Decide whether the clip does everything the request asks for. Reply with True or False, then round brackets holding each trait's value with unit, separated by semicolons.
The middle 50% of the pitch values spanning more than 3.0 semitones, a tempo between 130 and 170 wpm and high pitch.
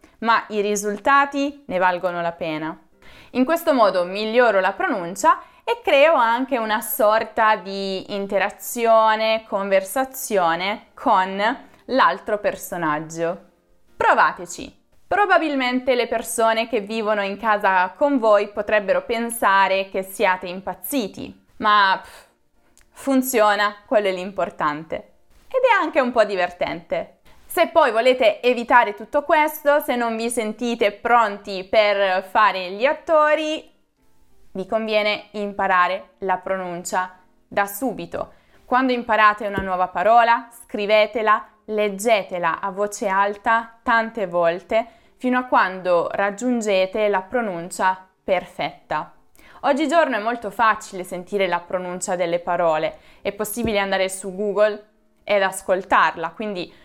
False (4.0 semitones; 115 wpm; 210 Hz)